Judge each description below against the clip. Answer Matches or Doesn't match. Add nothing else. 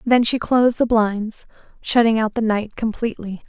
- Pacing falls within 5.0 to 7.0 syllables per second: Matches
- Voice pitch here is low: Doesn't match